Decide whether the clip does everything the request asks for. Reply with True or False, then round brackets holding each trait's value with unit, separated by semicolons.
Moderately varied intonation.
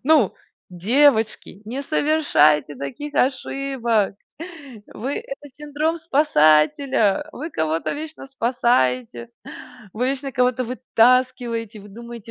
False (5.8 semitones)